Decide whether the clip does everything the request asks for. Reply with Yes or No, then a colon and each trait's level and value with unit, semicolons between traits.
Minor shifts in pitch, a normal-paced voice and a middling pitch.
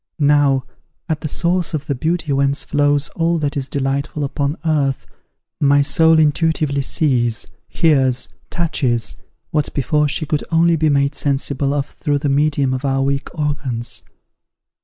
Yes: narrow, 2.0 semitones; average, 150 wpm; medium, 145 Hz